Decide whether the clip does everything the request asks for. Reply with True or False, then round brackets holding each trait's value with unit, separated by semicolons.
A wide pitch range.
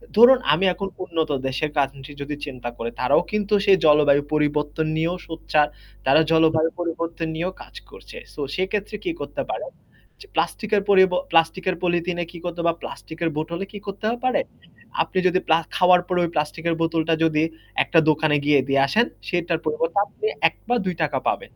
False (3.3 semitones)